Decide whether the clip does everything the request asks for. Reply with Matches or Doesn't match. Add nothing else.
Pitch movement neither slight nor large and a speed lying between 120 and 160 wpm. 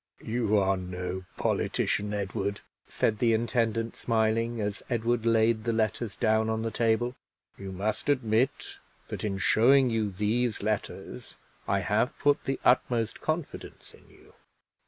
Doesn't match